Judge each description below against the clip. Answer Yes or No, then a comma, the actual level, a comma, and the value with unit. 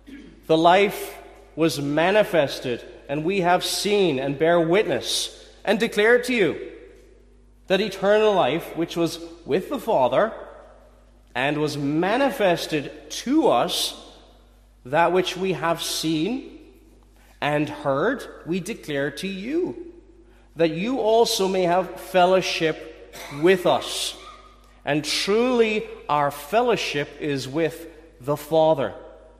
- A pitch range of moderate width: No, wide, 6.3 semitones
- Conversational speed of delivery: No, slow, 110 wpm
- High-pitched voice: No, medium, 175 Hz